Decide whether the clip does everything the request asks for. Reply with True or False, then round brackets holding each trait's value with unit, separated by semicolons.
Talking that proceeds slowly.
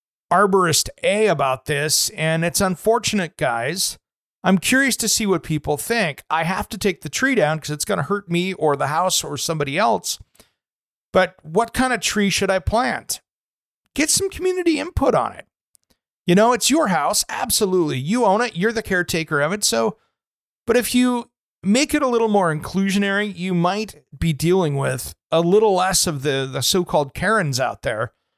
False (185 wpm)